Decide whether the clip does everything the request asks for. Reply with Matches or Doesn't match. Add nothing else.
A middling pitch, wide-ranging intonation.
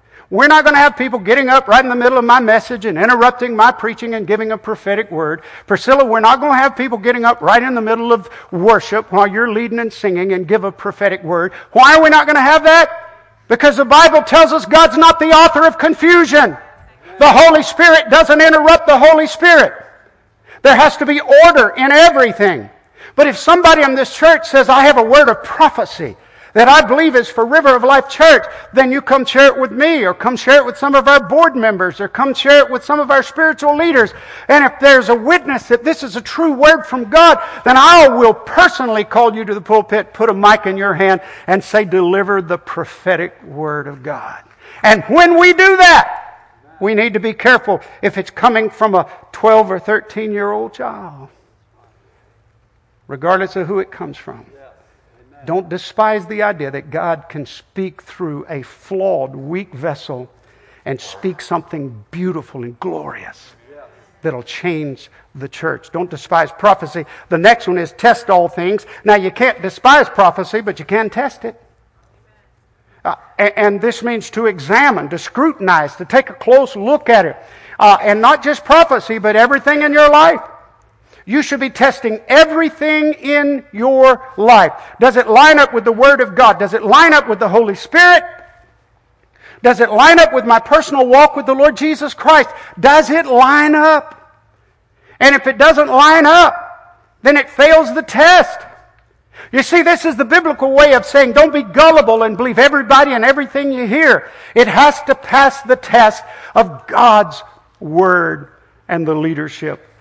Doesn't match